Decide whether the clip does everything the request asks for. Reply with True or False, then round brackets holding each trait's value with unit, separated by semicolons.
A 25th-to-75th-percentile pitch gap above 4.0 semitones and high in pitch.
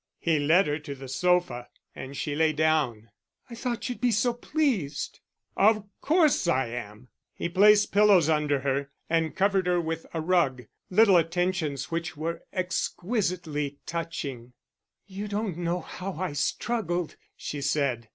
False (5.0 semitones; 165 Hz)